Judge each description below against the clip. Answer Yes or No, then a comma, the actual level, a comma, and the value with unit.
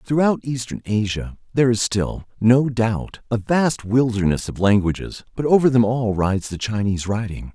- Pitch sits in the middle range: No, low, 115 Hz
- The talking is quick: No, average, 165 wpm